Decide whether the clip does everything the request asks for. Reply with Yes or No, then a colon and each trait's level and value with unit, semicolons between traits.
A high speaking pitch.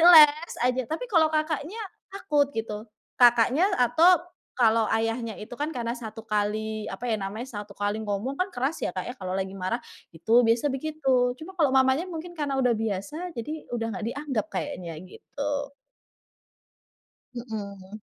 Yes: high, 245 Hz